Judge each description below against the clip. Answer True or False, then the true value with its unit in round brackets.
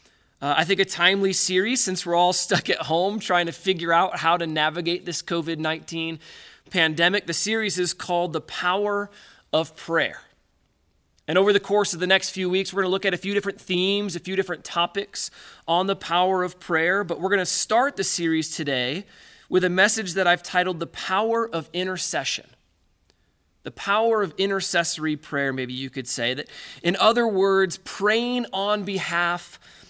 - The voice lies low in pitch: False (180 Hz)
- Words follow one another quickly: False (185 wpm)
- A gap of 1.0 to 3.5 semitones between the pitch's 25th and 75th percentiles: True (2.9 semitones)